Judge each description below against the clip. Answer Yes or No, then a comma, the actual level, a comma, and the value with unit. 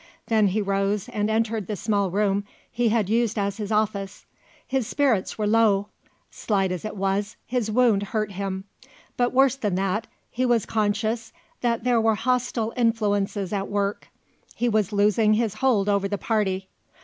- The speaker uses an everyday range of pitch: No, narrow, 2.3 semitones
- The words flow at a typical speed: Yes, average, 170 wpm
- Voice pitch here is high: Yes, high, 215 Hz